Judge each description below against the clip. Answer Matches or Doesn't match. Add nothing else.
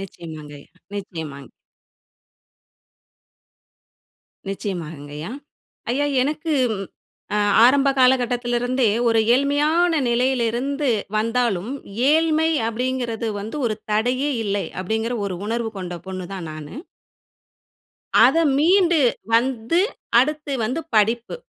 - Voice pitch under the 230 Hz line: Doesn't match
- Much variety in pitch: Matches